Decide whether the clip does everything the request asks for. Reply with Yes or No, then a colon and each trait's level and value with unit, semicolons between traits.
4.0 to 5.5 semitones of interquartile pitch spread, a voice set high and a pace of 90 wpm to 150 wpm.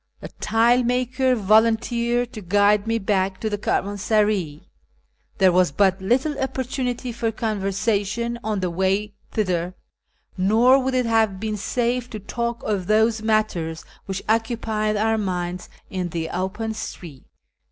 No: average, 3.5 semitones; high, 215 Hz; average, 145 wpm